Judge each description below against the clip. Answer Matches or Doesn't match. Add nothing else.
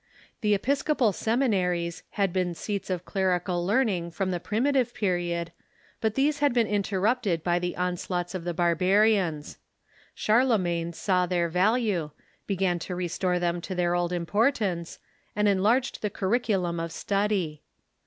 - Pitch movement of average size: Matches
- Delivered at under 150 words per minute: Matches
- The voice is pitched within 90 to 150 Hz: Doesn't match